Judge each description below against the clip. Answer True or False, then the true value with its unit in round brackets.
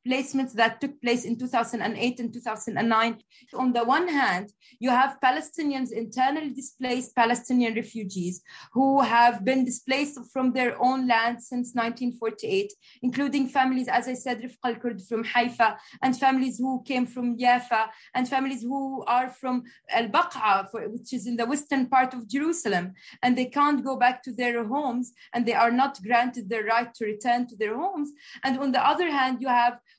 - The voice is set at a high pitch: True (250 Hz)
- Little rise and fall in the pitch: True (2.1 semitones)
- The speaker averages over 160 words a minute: True (170 wpm)